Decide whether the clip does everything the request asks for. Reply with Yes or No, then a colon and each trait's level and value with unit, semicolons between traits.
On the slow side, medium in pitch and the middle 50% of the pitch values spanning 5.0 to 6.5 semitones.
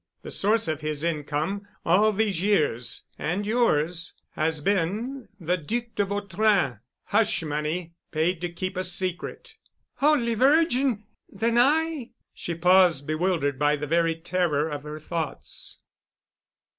Yes: slow, 120 wpm; medium, 180 Hz; average, 5.3 semitones